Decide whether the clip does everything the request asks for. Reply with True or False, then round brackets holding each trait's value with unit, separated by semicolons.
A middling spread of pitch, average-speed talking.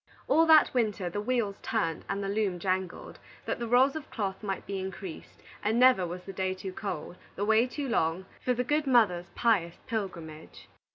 True (4.5 semitones; 190 wpm)